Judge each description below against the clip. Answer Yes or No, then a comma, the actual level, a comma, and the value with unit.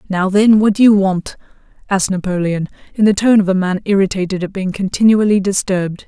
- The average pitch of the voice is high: Yes, high, 195 Hz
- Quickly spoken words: No, average, 190 wpm